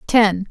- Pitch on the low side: No, high, 205 Hz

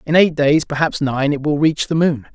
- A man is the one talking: Yes, male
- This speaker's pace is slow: No, fast, 230 wpm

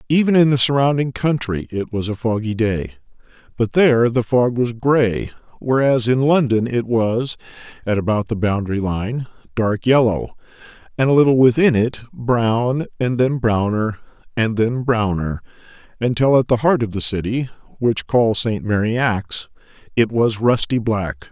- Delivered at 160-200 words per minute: No, average, 150 wpm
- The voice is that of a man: Yes, male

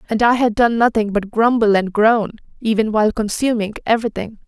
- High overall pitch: Yes, high, 220 Hz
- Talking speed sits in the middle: Yes, average, 190 wpm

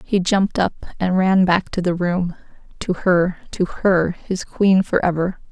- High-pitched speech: No, medium, 180 Hz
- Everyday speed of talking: Yes, average, 175 wpm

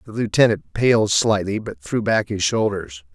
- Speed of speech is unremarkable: Yes, average, 170 wpm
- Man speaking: Yes, male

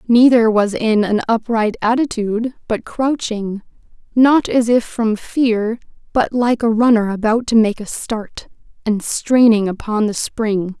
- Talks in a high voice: Yes, high, 225 Hz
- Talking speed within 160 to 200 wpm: No, average, 145 wpm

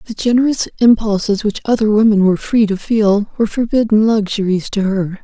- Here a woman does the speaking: Yes, female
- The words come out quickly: No, average, 170 wpm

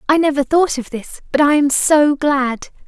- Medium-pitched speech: No, very high, 285 Hz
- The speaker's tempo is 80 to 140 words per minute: No, fast, 210 wpm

